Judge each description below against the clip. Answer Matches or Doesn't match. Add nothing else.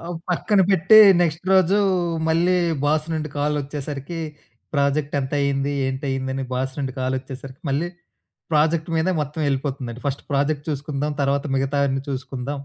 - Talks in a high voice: Doesn't match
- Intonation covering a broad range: Doesn't match